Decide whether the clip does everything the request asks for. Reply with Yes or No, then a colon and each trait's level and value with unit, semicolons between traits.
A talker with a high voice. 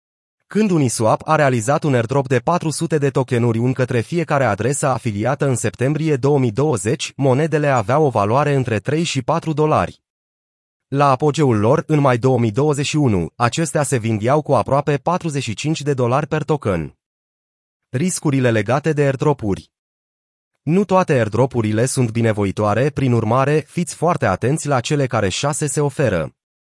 No: low, 135 Hz